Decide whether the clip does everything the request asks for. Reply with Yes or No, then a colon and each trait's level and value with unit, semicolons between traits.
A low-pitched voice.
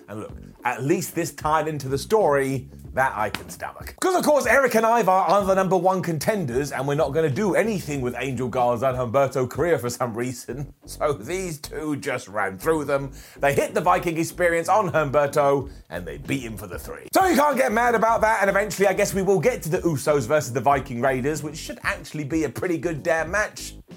No: medium, 160 Hz